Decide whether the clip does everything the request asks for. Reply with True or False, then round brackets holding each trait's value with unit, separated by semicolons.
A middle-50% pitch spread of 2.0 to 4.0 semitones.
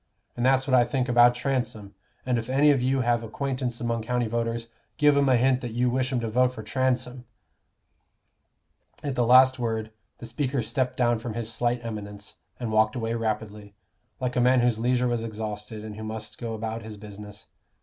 True (2.4 semitones)